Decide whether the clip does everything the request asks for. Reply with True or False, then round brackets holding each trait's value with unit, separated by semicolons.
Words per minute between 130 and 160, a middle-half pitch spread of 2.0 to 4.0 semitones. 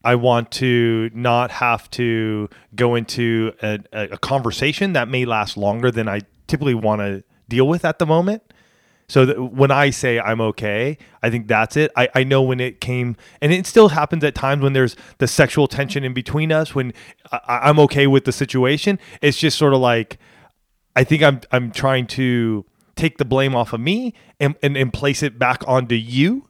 False (200 wpm; 3.6 semitones)